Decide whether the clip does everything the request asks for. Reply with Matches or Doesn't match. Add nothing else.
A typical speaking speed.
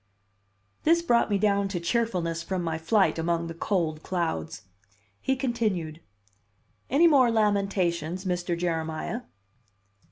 Doesn't match